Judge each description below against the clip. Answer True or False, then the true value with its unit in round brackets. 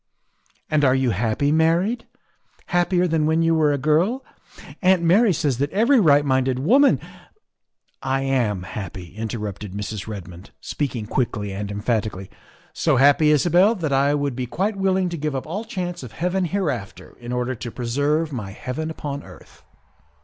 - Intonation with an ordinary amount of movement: False (6.5 semitones)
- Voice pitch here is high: False (145 Hz)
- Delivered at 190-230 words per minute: False (170 wpm)